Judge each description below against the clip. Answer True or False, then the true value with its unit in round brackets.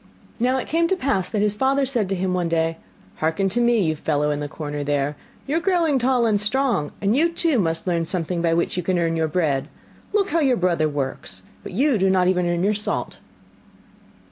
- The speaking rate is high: True (225 wpm)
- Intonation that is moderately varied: False (7.6 semitones)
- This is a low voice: False (185 Hz)